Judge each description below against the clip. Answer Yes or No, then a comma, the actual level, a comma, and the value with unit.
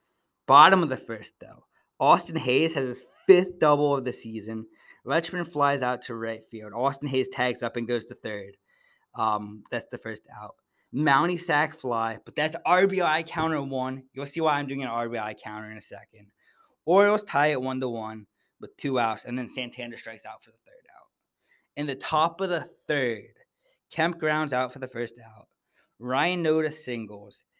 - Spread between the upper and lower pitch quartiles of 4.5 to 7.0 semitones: Yes, wide, 5.4 semitones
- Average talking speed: Yes, average, 185 wpm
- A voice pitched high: No, low, 130 Hz